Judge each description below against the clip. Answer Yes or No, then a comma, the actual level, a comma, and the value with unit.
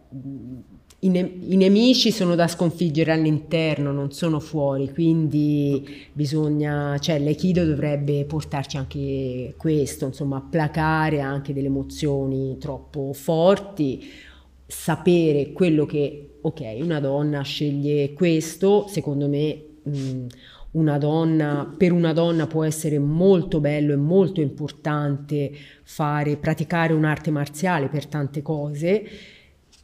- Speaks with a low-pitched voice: No, medium, 150 Hz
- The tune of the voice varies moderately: No, narrow, 2.3 semitones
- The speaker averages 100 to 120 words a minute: Yes, slow, 115 wpm